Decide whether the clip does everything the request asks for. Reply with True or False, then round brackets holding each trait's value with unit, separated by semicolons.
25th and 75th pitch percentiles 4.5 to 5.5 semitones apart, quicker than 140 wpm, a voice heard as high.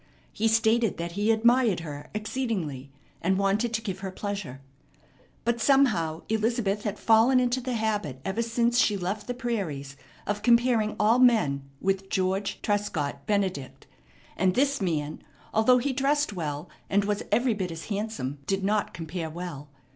True (4.8 semitones; 155 wpm; 205 Hz)